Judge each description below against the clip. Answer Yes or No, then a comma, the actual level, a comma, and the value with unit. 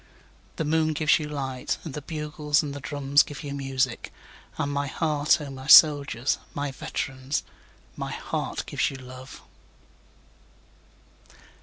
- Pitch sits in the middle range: Yes, medium, 145 Hz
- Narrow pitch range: Yes, narrow, 2.0 semitones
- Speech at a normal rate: No, slow, 125 wpm